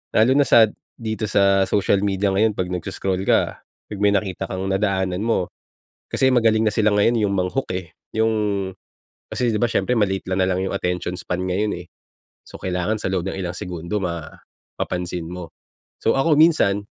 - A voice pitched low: Yes, low, 100 Hz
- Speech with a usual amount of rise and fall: Yes, average, 3.1 semitones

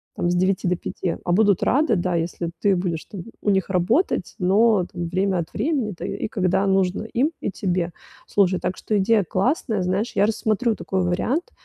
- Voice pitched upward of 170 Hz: Yes, high, 190 Hz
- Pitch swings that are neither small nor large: Yes, average, 3.2 semitones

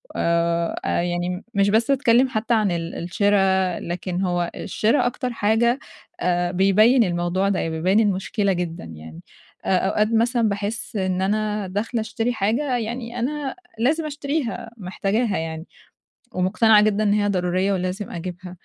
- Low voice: No, high, 200 Hz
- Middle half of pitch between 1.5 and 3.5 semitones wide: No, average, 4.1 semitones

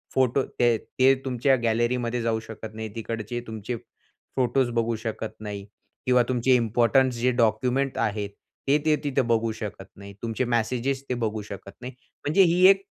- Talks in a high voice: No, low, 120 Hz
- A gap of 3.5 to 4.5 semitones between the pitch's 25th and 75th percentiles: No, average, 2.8 semitones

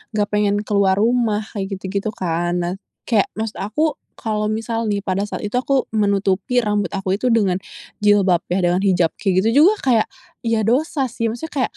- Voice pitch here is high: Yes, high, 210 Hz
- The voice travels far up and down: No, average, 2.8 semitones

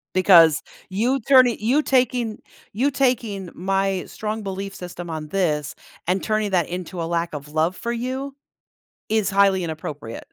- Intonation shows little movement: No, average, 5.0 semitones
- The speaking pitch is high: Yes, high, 195 Hz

